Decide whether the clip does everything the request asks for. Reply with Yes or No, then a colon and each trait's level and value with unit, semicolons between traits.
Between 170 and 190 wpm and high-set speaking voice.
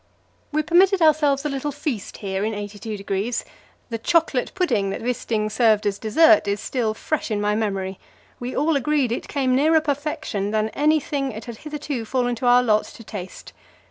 Yes: average, 180 wpm; high, 245 Hz